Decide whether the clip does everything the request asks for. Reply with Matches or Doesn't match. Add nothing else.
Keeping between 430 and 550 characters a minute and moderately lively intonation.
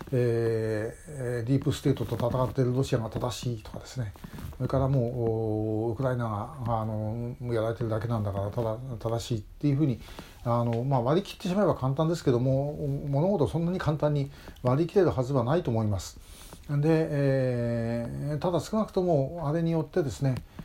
Doesn't match